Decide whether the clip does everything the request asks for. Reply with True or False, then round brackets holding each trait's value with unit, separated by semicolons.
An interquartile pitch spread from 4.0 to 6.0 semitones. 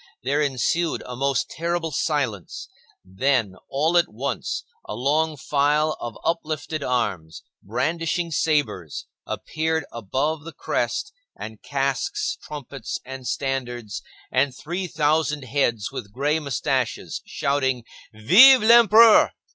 True (4.4 semitones)